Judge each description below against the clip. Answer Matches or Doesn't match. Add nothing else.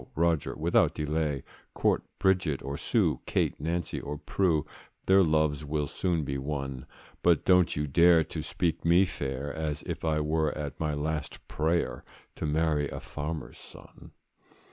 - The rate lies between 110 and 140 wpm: Doesn't match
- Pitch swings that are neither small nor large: Doesn't match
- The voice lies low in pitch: Matches